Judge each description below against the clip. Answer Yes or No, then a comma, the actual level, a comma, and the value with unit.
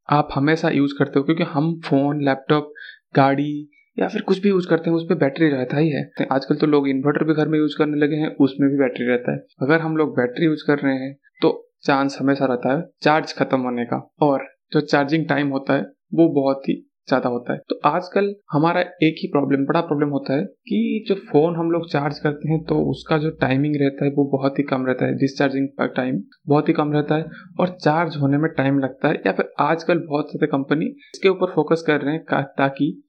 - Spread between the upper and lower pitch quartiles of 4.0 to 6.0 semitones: No, average, 2.9 semitones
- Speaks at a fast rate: Yes, fast, 225 wpm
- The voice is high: No, medium, 150 Hz